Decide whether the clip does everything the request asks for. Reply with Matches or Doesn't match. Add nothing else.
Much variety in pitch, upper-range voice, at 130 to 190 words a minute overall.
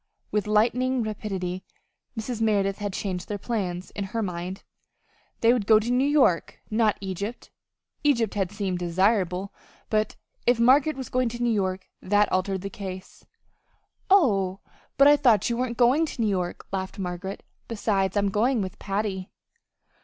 Doesn't match